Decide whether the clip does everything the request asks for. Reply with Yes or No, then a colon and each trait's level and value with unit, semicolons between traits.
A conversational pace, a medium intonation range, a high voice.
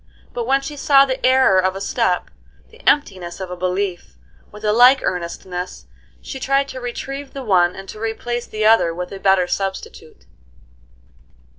No: average, 170 wpm; wide, 6.0 semitones; high, 215 Hz